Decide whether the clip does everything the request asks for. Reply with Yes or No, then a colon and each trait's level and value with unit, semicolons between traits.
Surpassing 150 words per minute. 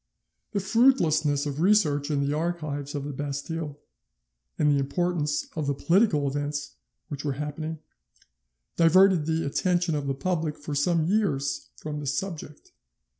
No: average, 145 wpm